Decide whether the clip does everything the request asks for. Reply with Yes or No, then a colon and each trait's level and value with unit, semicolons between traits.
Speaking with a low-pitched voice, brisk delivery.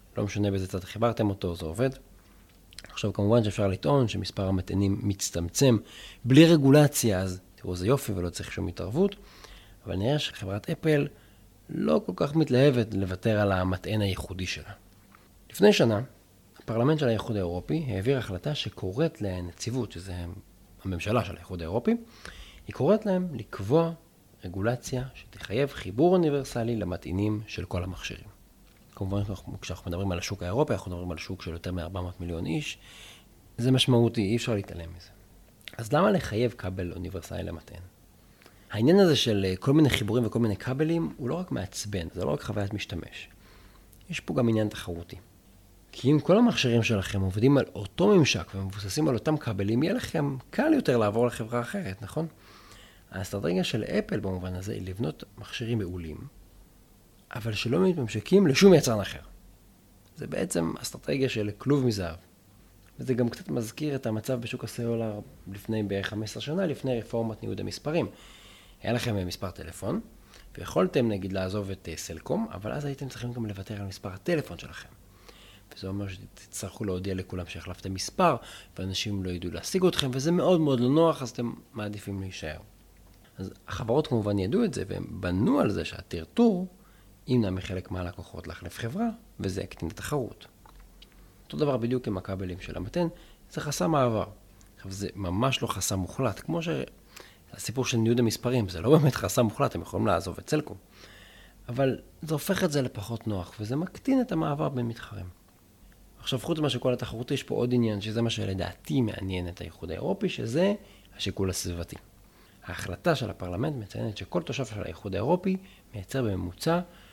Yes: low, 105 Hz; fast, 160 wpm